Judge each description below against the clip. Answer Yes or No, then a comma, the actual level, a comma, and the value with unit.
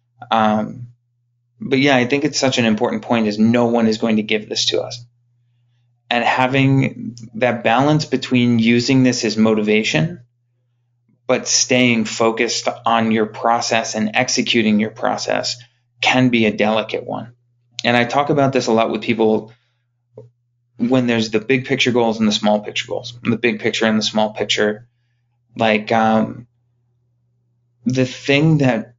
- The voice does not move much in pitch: Yes, narrow, 1.8 semitones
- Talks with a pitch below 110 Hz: No, low, 120 Hz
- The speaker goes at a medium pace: Yes, average, 155 wpm